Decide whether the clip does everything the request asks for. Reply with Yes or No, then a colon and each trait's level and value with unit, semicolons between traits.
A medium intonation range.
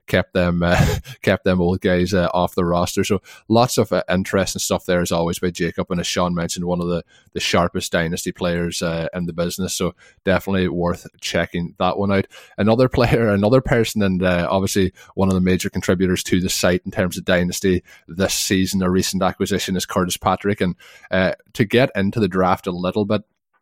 No: narrow, 1.7 semitones